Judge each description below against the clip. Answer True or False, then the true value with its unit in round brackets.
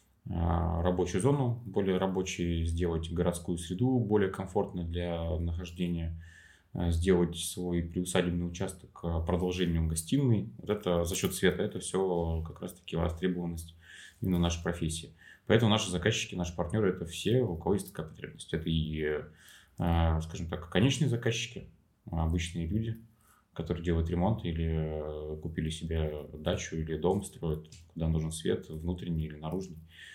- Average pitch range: False (2.1 semitones)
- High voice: False (85 Hz)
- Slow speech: False (135 wpm)